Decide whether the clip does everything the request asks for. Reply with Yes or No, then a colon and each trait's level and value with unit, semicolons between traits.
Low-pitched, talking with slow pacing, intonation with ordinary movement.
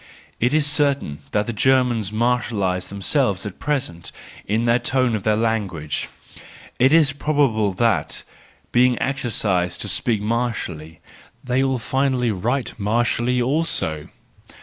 Yes: low, 120 Hz; slow, 125 wpm; average, 4.4 semitones